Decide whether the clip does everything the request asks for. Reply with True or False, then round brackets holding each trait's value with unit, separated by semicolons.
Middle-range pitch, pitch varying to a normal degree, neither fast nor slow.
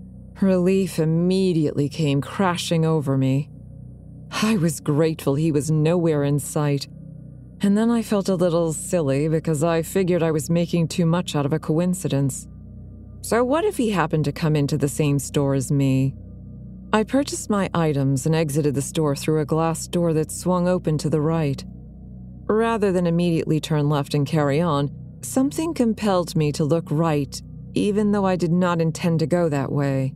True (160 Hz; 3.6 semitones; 175 wpm)